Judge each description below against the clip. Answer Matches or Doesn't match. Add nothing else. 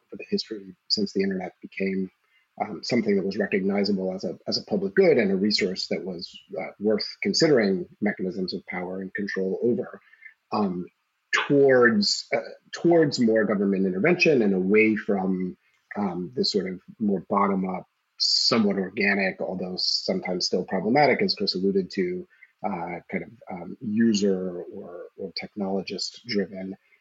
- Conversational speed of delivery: Matches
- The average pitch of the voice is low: Matches